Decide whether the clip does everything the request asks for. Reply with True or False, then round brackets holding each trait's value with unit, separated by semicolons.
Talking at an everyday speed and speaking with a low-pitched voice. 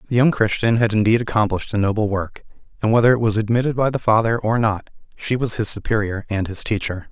False (220 wpm; 110 Hz)